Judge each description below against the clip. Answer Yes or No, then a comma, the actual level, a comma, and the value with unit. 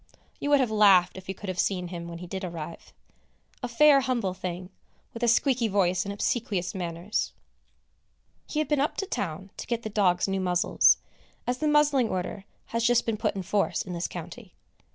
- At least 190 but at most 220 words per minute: Yes, average, 200 wpm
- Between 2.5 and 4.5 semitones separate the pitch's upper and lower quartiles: No, average, 5.0 semitones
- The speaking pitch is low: No, high, 200 Hz